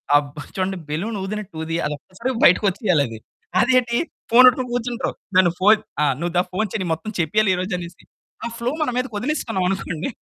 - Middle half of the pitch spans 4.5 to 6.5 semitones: Yes, average, 5.1 semitones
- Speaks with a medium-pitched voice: No, high, 195 Hz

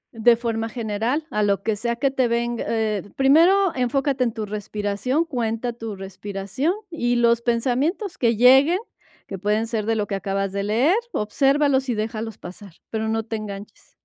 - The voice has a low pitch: No, high, 230 Hz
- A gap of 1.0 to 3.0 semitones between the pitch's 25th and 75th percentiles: No, average, 3.5 semitones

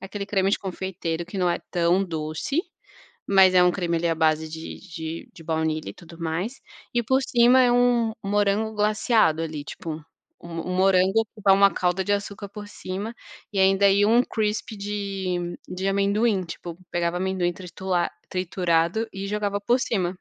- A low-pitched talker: No, high, 190 Hz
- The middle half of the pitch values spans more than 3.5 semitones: No, average, 3.2 semitones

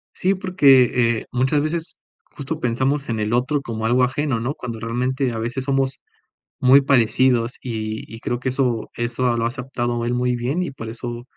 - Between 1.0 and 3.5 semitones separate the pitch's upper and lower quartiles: Yes, narrow, 2.4 semitones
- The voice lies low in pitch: Yes, low, 125 Hz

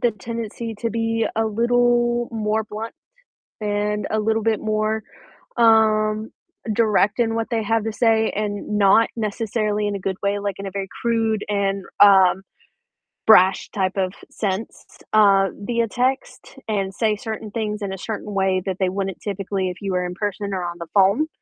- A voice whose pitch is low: No, high, 210 Hz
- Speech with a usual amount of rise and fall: No, narrow, 2.2 semitones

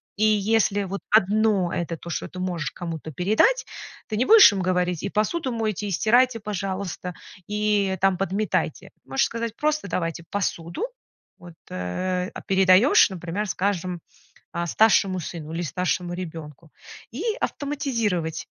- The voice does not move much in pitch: No, average, 3.6 semitones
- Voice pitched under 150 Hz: No, high, 190 Hz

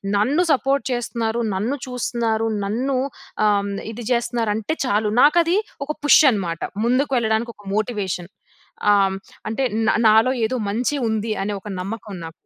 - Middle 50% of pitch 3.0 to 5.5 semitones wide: Yes, average, 3.4 semitones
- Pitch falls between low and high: No, high, 225 Hz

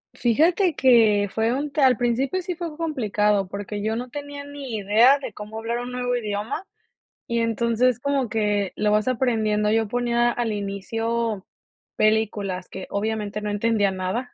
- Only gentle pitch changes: No, average, 3.3 semitones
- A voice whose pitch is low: No, high, 225 Hz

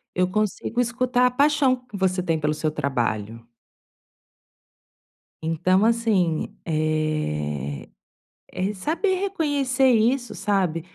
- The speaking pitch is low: No, high, 190 Hz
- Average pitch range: No, wide, 8.1 semitones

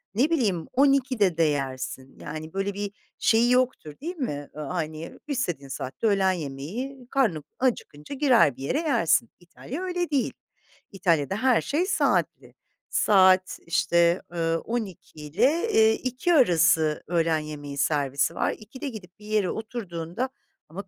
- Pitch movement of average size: No, wide, 8.1 semitones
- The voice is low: No, high, 190 Hz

